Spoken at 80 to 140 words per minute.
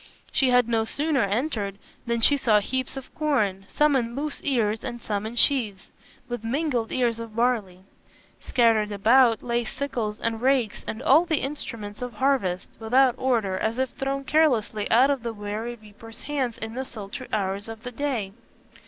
No: average, 175 wpm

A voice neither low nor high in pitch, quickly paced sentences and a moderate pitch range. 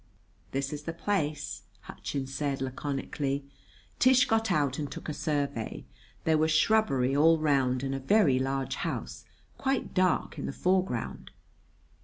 No: medium, 145 Hz; average, 145 wpm; average, 3.7 semitones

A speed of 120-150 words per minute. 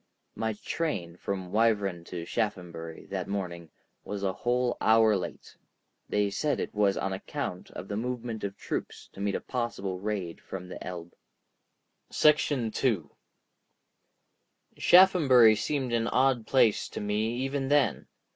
Yes: average, 140 wpm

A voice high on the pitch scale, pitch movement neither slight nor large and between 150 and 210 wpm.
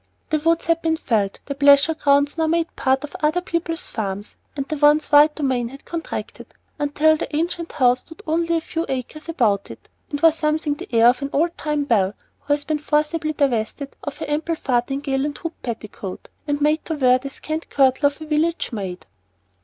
Yes: very high, 295 Hz; average, 3.1 semitones; fast, 205 wpm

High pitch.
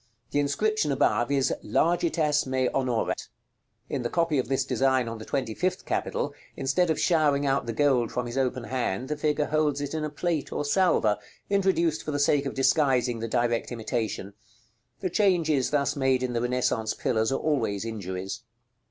No: low, 135 Hz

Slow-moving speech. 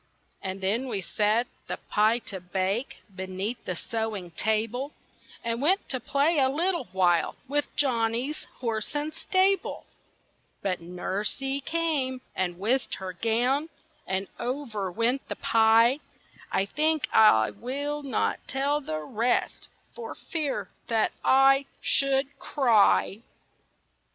Yes: slow, 115 wpm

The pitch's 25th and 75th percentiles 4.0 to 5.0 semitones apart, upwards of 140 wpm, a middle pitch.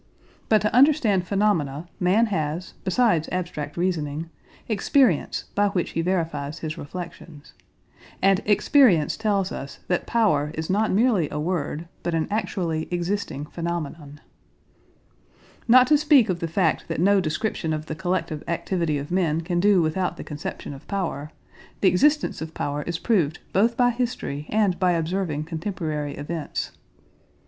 Yes: average, 4.5 semitones; average, 150 wpm; medium, 175 Hz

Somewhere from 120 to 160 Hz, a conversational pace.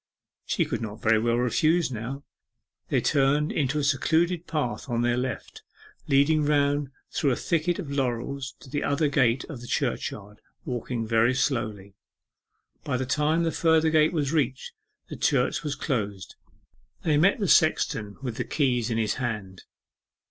Yes: low, 135 Hz; average, 165 wpm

